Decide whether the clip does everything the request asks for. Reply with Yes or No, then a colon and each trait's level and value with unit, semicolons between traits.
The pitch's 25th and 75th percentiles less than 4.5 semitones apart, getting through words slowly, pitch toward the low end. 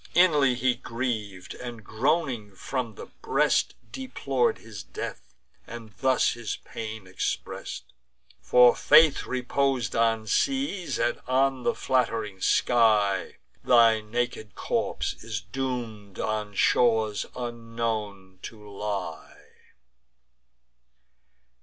Yes: average, 3.3 semitones; slow, 100 wpm; low, 115 Hz